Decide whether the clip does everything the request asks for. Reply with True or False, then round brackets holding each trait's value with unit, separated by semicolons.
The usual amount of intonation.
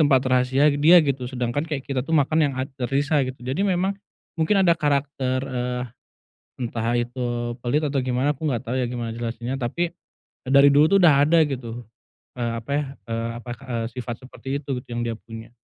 True (3.1 semitones)